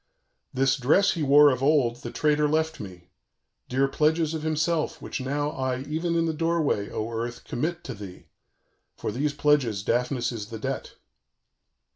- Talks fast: No, average, 170 wpm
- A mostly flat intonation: No, average, 4.4 semitones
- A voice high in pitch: No, medium, 140 Hz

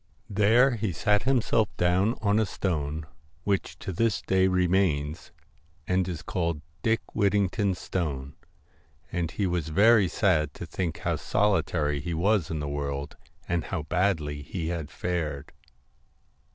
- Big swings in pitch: No, average, 4.5 semitones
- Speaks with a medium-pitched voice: No, very low, 90 Hz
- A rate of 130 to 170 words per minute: Yes, average, 150 wpm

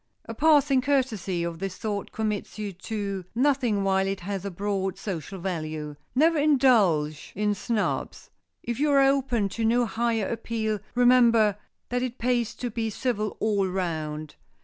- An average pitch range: Yes, average, 4.3 semitones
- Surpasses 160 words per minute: No, average, 155 wpm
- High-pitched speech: Yes, high, 215 Hz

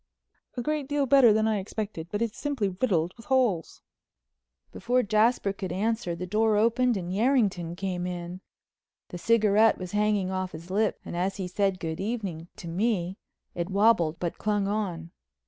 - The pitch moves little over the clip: No, average, 3.9 semitones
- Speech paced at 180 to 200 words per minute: No, average, 170 wpm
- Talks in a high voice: Yes, high, 200 Hz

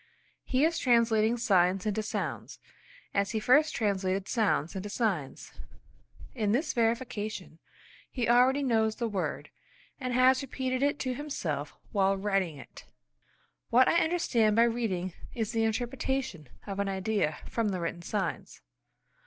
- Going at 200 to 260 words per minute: No, average, 140 wpm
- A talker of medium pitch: No, high, 220 Hz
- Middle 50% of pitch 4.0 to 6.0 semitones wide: Yes, average, 4.4 semitones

